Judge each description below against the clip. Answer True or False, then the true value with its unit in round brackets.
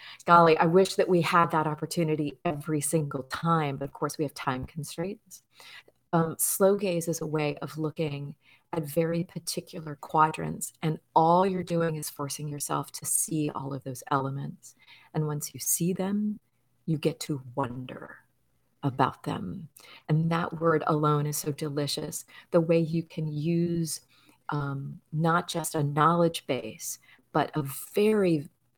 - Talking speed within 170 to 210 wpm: False (155 wpm)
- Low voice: False (155 Hz)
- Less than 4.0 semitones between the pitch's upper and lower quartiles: True (2.5 semitones)